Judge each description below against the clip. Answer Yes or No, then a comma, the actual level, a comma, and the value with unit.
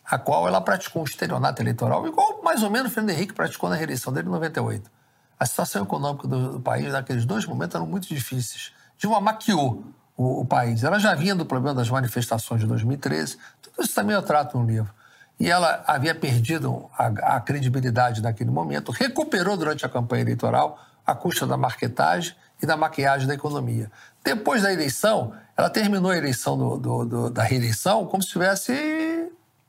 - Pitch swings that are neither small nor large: No, wide, 7.6 semitones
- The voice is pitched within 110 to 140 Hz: Yes, low, 135 Hz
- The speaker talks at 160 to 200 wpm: Yes, fast, 185 wpm